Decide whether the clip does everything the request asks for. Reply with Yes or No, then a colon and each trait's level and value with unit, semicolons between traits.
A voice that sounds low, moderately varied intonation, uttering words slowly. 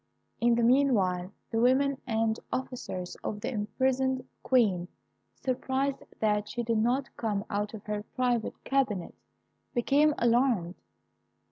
No: high, 235 Hz; average, 4.0 semitones; slow, 125 wpm